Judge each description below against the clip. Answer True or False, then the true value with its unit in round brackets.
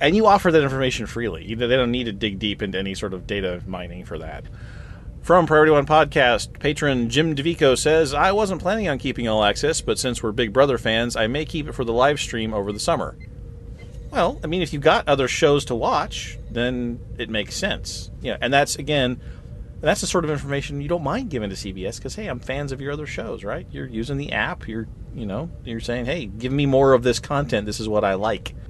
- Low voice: True (125 Hz)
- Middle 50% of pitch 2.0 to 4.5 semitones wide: False (4.9 semitones)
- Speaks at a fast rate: True (235 wpm)